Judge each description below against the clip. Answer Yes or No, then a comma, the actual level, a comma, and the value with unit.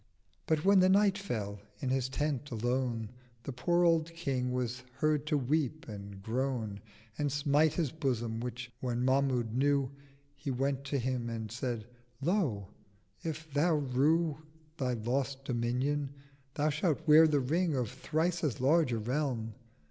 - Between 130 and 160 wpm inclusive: Yes, average, 155 wpm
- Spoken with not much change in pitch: No, average, 3.9 semitones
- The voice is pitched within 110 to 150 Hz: Yes, low, 135 Hz